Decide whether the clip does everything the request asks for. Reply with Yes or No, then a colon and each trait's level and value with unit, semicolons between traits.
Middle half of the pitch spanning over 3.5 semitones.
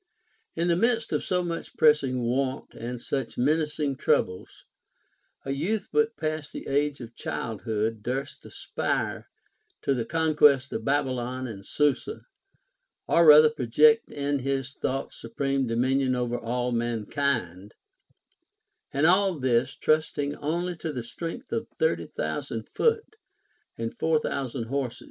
Yes: average, 4.1 semitones